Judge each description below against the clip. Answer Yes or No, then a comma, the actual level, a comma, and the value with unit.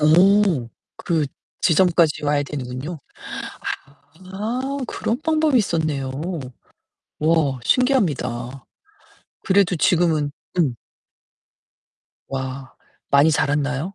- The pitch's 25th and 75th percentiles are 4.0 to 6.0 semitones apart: Yes, wide, 5.5 semitones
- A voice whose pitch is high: No, medium, 155 Hz